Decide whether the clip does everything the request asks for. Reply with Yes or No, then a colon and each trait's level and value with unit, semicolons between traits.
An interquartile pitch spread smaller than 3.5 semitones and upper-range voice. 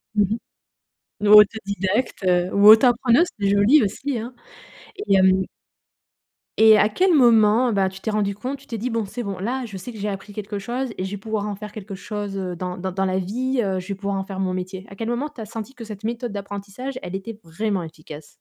Yes: average, 3.1 semitones; high, 205 Hz